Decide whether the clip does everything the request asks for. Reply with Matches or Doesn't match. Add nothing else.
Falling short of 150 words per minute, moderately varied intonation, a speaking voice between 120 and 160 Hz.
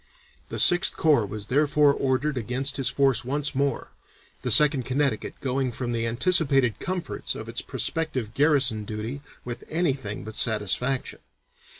Matches